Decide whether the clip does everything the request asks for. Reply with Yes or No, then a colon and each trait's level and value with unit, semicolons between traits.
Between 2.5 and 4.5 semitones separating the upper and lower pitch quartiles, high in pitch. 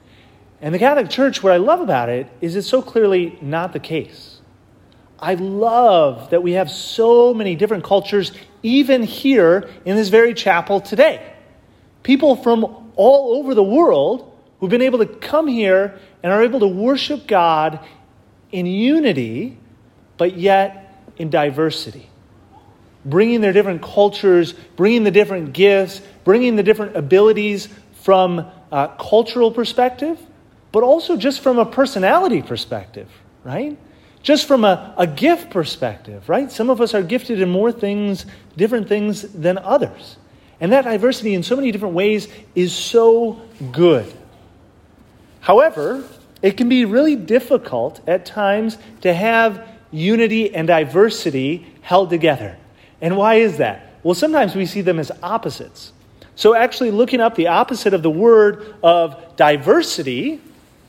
No: wide, 5.5 semitones; high, 200 Hz